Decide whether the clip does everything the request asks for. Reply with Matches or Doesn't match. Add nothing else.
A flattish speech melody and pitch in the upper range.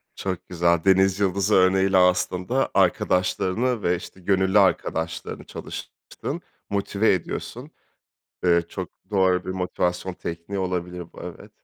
Doesn't match